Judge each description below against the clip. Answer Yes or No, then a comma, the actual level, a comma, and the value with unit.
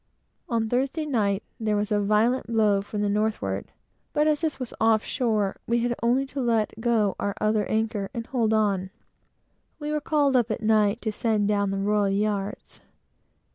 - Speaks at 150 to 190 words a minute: Yes, average, 180 wpm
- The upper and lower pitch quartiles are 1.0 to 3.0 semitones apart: Yes, narrow, 2.6 semitones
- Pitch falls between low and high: No, high, 220 Hz